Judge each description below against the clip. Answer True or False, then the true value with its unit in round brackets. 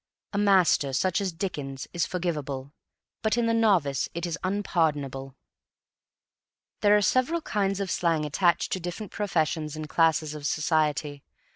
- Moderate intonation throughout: True (4.8 semitones)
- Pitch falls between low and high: True (170 Hz)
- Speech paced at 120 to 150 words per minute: True (145 wpm)